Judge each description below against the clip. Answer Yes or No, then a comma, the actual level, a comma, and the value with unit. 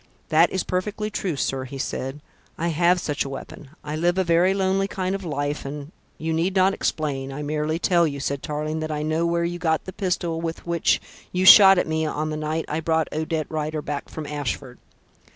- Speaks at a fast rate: Yes, fast, 220 wpm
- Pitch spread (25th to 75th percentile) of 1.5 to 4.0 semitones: Yes, average, 2.9 semitones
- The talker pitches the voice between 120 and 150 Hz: No, medium, 160 Hz